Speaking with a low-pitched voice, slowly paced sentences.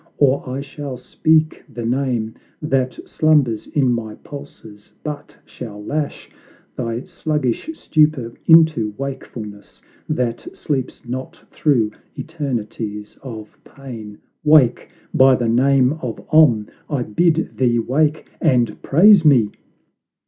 Yes: low, 130 Hz; slow, 115 wpm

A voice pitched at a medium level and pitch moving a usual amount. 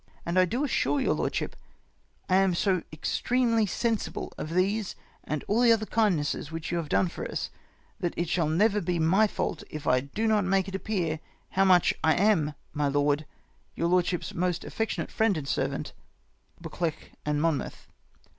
Yes: medium, 180 Hz; average, 4.8 semitones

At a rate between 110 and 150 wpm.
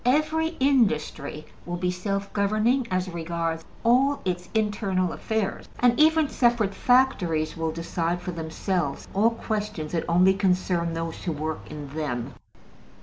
Yes: average, 140 wpm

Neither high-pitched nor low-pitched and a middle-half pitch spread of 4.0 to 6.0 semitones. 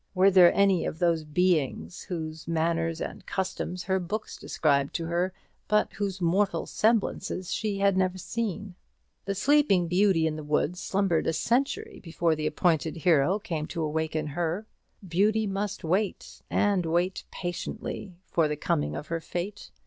No: medium, 175 Hz; average, 3.5 semitones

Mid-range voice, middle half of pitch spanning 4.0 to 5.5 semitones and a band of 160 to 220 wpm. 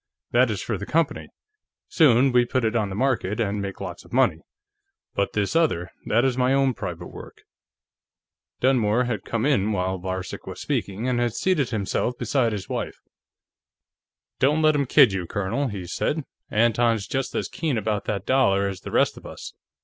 No: low, 115 Hz; average, 4.8 semitones; average, 185 wpm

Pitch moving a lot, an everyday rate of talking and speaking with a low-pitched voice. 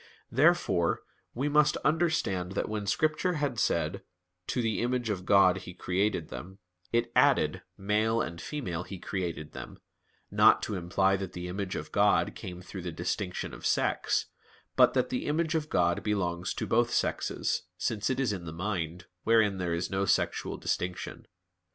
No: average, 4.9 semitones; average, 170 wpm; low, 100 Hz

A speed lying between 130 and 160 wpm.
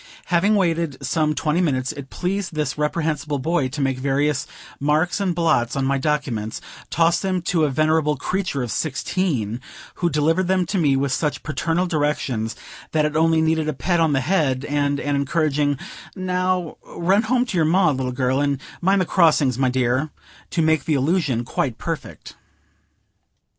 No: average, 175 wpm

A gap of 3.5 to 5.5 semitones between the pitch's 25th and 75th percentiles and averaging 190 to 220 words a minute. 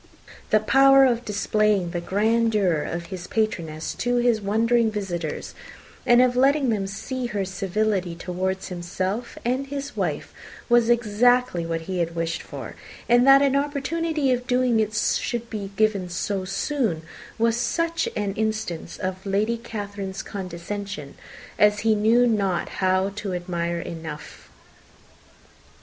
No: average, 4.4 semitones; average, 140 wpm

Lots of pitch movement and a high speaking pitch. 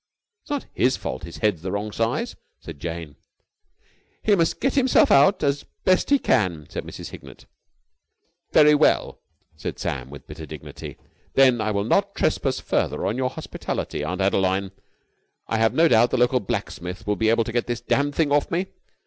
No: wide, 7.1 semitones; low, 115 Hz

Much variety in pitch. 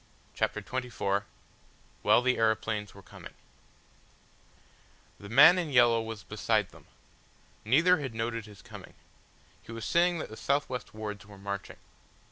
No: average, 3.7 semitones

